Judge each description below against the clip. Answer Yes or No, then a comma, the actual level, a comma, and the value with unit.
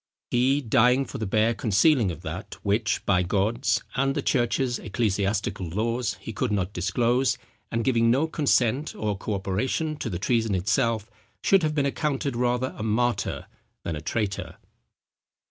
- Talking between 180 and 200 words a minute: No, average, 160 wpm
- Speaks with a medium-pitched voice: No, low, 115 Hz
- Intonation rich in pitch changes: No, average, 4.2 semitones